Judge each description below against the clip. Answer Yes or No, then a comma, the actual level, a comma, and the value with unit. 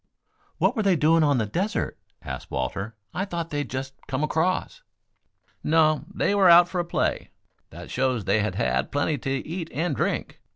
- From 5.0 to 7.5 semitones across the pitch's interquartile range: Yes, wide, 5.4 semitones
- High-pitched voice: No, medium, 155 Hz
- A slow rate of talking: No, average, 190 wpm